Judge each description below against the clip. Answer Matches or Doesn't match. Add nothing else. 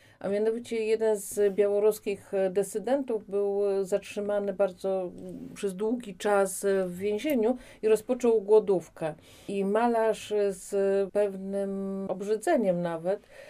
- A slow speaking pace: Matches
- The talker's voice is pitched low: Doesn't match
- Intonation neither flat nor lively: Doesn't match